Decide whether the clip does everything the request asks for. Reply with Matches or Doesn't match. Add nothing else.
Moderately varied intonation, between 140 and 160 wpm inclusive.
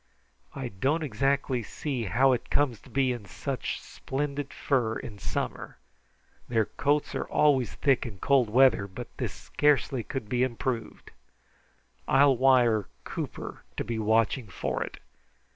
Matches